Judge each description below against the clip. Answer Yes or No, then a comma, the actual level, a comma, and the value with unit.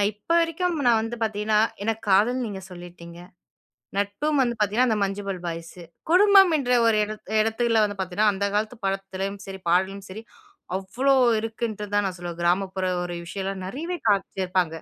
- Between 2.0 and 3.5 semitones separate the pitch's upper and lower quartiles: Yes, average, 3.2 semitones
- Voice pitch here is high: Yes, high, 205 Hz